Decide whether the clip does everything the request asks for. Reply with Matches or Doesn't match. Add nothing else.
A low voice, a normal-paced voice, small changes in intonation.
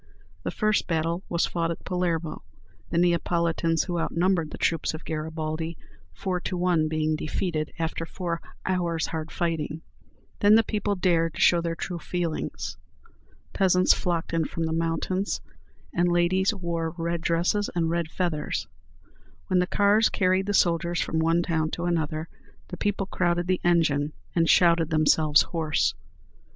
Doesn't match